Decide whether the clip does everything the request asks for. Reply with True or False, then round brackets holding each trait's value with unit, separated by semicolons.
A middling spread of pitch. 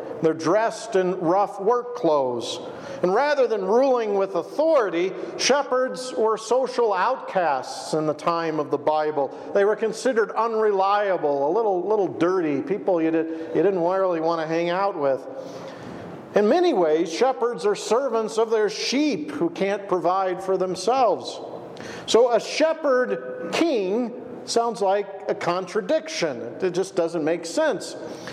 False (6.2 semitones)